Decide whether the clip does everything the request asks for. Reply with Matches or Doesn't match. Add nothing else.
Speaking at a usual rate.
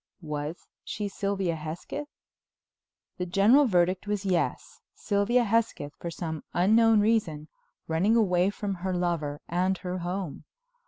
Doesn't match